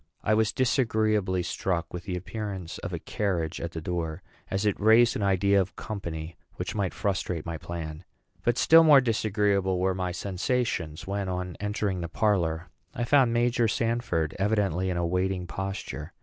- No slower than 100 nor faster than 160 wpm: No, average, 170 wpm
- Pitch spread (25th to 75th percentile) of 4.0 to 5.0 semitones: No, average, 3.6 semitones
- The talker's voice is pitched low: Yes, very low, 95 Hz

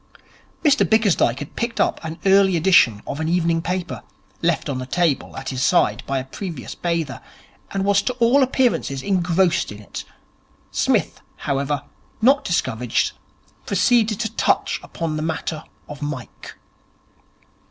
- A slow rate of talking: No, average, 145 wpm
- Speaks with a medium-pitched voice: Yes, medium, 170 Hz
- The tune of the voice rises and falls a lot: Yes, wide, 6.1 semitones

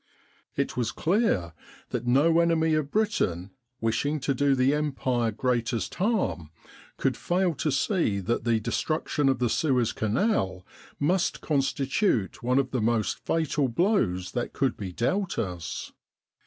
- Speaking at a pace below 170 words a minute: Yes, average, 140 wpm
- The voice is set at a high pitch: No, low, 130 Hz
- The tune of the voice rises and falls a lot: Yes, wide, 5.9 semitones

